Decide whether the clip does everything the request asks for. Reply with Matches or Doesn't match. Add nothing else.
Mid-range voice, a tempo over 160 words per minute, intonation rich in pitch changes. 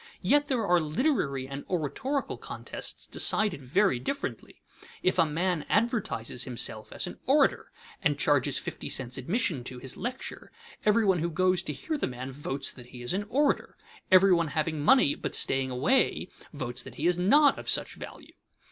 Matches